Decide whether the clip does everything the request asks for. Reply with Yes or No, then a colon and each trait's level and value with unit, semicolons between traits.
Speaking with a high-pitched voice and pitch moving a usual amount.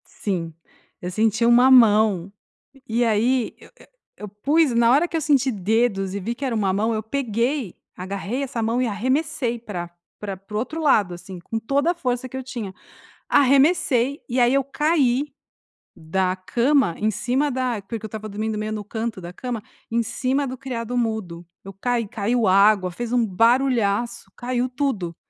Yes: high, 230 Hz; average, 4.0 semitones